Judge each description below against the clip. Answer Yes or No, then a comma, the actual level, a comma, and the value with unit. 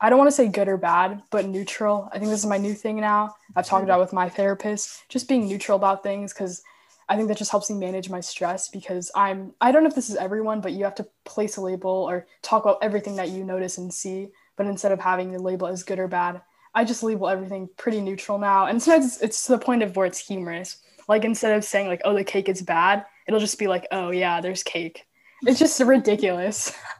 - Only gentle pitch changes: Yes, narrow, 2.3 semitones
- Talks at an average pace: No, fast, 250 wpm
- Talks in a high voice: Yes, high, 200 Hz